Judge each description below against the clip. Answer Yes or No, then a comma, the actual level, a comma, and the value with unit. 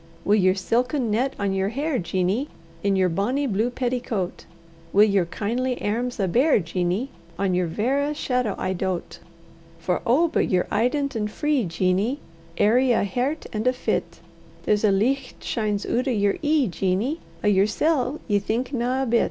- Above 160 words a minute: Yes, average, 175 wpm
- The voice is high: Yes, high, 225 Hz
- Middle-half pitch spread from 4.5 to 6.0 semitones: Yes, average, 4.9 semitones